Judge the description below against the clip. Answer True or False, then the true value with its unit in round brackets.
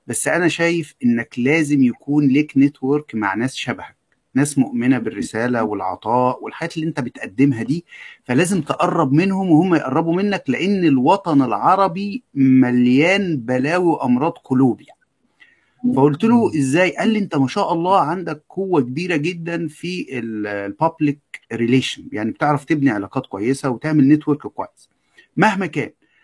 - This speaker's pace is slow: False (135 wpm)